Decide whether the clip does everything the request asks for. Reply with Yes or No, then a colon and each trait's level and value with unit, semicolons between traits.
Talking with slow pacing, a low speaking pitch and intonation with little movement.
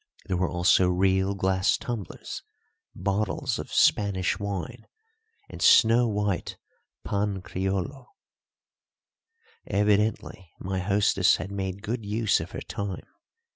Yes: slow, 110 wpm; low, 100 Hz; narrow, 1.8 semitones